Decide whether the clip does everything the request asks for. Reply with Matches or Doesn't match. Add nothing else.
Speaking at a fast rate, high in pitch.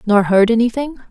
Doesn't match